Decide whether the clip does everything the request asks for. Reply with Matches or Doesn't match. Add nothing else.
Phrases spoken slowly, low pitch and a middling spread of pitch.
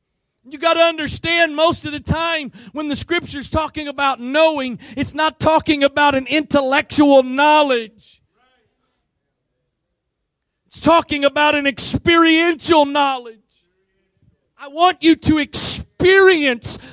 Doesn't match